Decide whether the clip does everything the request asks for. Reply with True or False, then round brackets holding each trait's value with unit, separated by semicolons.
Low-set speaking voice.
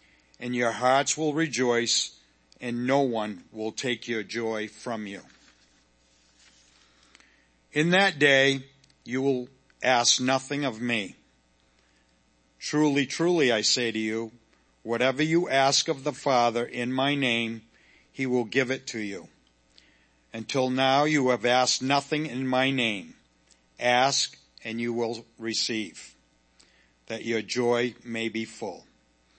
True (115 Hz)